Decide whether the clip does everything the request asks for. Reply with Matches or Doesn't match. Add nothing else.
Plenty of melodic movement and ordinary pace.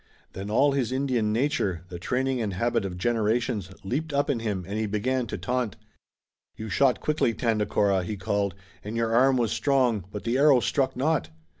Doesn't match